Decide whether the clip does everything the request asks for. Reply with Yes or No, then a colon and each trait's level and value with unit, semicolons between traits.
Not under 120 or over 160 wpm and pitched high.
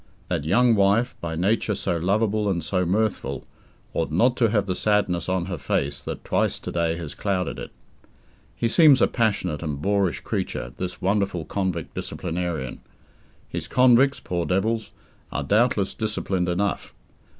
No: average, 155 wpm; very low, 95 Hz